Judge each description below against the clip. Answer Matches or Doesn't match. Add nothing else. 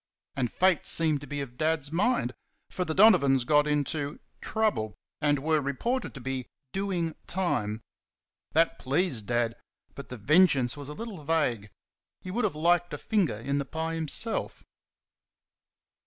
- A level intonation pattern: Doesn't match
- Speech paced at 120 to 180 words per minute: Matches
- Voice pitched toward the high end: Doesn't match